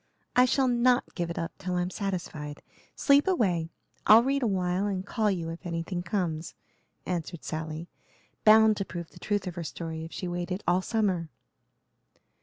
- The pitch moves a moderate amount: Yes, average, 4.1 semitones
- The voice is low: No, medium, 180 Hz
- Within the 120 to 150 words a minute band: No, average, 170 wpm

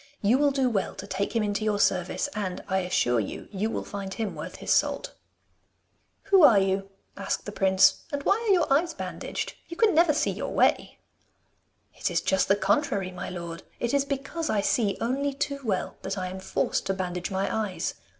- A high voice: Yes, high, 205 Hz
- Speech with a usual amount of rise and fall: No, wide, 6.5 semitones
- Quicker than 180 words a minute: Yes, fast, 205 wpm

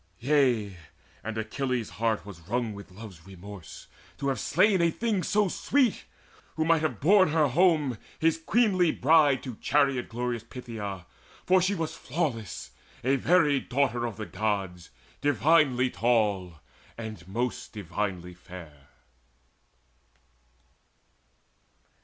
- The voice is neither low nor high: No, low, 125 Hz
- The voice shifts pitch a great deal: Yes, wide, 7.2 semitones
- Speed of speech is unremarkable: No, slow, 125 wpm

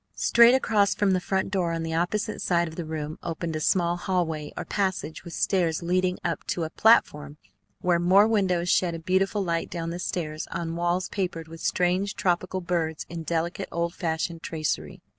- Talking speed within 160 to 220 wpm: Yes, average, 190 wpm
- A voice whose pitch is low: No, medium, 175 Hz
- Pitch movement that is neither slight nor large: No, narrow, 2.2 semitones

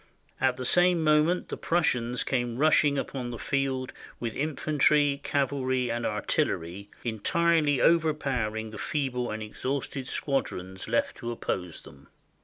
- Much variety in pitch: No, average, 4.3 semitones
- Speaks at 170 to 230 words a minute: No, slow, 135 wpm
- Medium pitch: No, low, 130 Hz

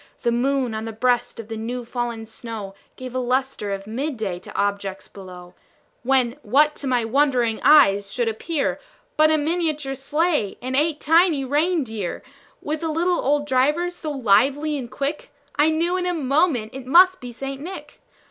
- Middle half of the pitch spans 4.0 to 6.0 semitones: Yes, average, 5.1 semitones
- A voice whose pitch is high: Yes, very high, 265 Hz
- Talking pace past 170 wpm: Yes, average, 180 wpm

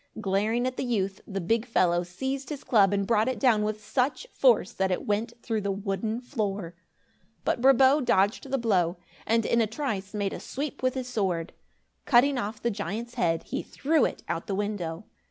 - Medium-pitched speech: No, high, 215 Hz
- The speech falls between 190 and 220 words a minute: Yes, average, 195 wpm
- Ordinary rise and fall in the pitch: Yes, average, 4.2 semitones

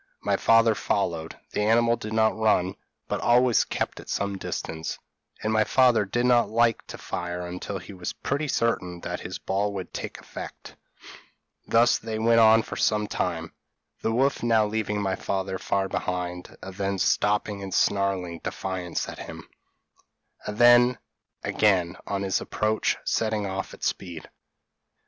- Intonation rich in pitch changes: No, average, 3.2 semitones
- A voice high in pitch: No, low, 105 Hz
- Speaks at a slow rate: No, average, 160 wpm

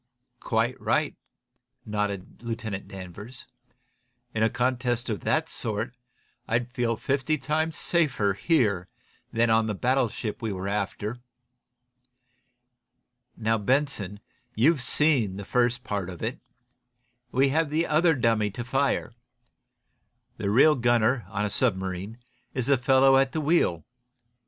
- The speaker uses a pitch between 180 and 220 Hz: No, low, 120 Hz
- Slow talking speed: Yes, slow, 125 wpm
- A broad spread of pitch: No, average, 4.4 semitones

